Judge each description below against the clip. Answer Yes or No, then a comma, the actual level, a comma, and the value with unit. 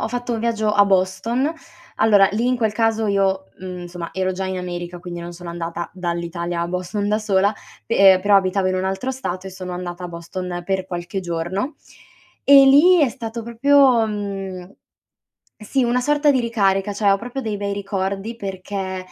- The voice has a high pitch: Yes, high, 195 Hz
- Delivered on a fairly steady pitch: No, average, 3.7 semitones